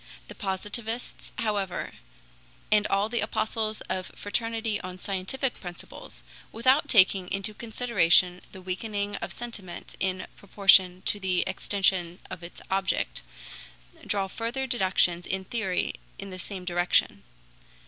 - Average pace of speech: No, slow, 125 wpm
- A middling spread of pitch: Yes, average, 3.1 semitones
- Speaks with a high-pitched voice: Yes, high, 195 Hz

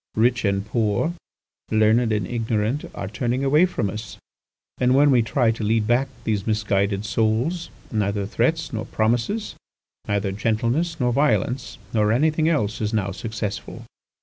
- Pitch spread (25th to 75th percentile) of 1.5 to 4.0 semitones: Yes, average, 3.1 semitones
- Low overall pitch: Yes, low, 110 Hz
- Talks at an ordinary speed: Yes, average, 150 wpm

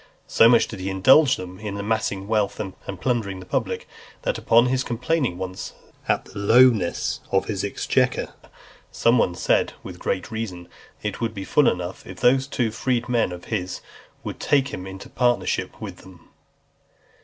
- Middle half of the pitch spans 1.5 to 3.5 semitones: No, average, 4.6 semitones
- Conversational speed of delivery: Yes, average, 175 wpm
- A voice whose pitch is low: Yes, low, 110 Hz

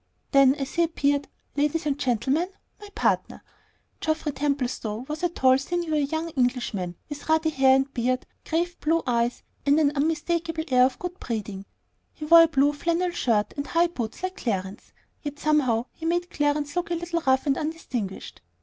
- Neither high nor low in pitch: No, very high, 290 Hz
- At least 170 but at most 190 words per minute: Yes, average, 175 wpm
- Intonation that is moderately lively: Yes, average, 4.2 semitones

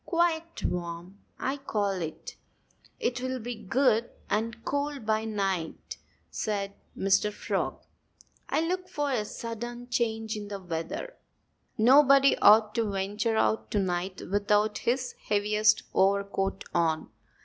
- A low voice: No, high, 215 Hz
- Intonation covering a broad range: No, average, 4.0 semitones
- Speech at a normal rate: No, slow, 125 wpm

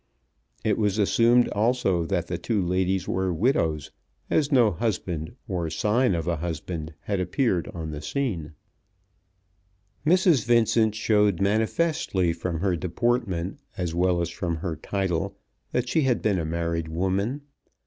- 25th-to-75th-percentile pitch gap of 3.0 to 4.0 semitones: No, average, 5.3 semitones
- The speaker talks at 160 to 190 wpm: No, average, 145 wpm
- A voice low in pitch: Yes, very low, 95 Hz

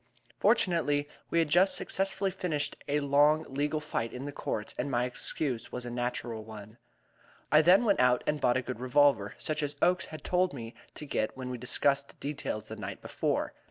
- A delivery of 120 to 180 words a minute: No, average, 195 wpm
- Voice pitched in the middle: Yes, medium, 145 Hz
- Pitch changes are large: No, average, 4.1 semitones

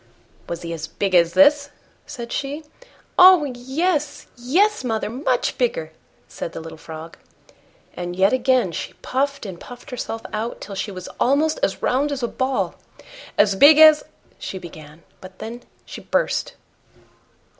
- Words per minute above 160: No, average, 155 wpm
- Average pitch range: No, wide, 7.4 semitones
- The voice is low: No, high, 240 Hz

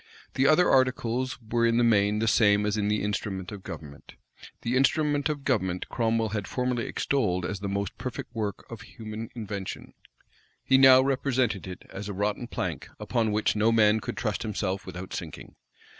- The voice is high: No, low, 110 Hz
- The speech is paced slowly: No, average, 180 wpm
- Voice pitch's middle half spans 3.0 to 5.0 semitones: Yes, average, 3.6 semitones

